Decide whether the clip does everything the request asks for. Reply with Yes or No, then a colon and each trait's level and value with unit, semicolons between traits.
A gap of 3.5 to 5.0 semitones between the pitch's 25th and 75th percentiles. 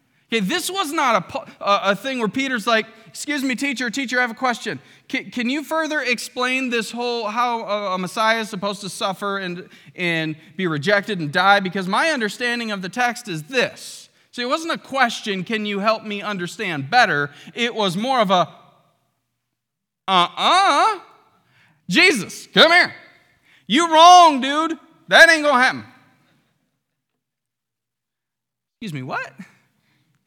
No: wide, 5.6 semitones